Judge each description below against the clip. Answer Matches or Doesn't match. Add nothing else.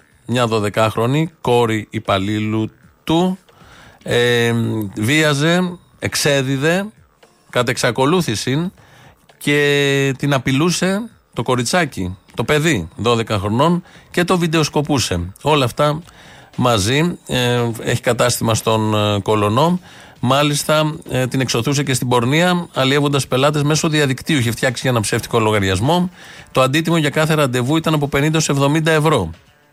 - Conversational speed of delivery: Doesn't match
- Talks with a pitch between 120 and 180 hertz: Matches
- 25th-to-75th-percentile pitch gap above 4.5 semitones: Matches